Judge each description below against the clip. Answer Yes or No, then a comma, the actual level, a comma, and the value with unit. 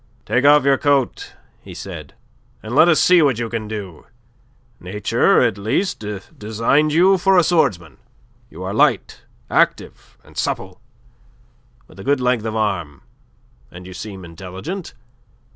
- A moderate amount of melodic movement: No, wide, 7.3 semitones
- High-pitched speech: No, low, 115 Hz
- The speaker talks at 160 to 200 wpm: No, average, 145 wpm